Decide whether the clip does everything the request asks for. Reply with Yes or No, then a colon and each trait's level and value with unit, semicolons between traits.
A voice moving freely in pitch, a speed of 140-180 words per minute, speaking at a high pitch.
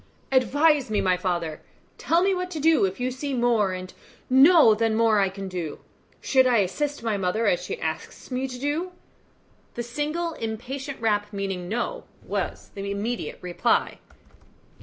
Yes: wide, 6.2 semitones; average, 165 wpm; high, 230 Hz